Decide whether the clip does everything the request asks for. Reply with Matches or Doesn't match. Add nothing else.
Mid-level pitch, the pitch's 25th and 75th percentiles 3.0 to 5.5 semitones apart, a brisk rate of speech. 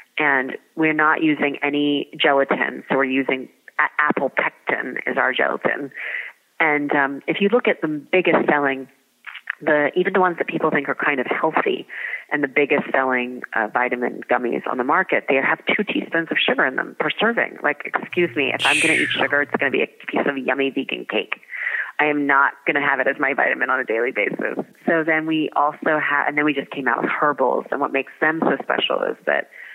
Doesn't match